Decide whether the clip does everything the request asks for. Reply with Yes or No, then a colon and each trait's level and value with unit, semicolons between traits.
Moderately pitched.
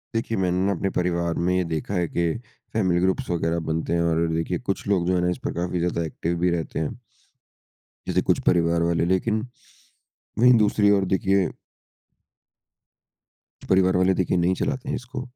No: very low, 90 Hz